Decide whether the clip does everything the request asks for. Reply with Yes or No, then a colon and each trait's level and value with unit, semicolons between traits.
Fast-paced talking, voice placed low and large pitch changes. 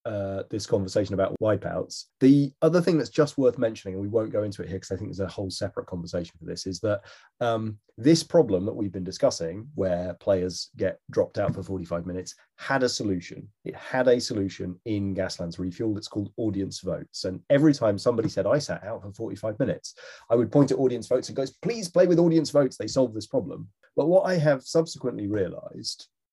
Yes: fast, 215 wpm; low, 110 Hz; wide, 6.4 semitones